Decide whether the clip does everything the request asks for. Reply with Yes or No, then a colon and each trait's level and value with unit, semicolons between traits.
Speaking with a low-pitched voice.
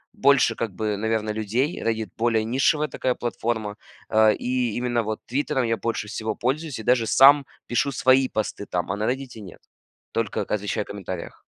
Yes: low, 115 Hz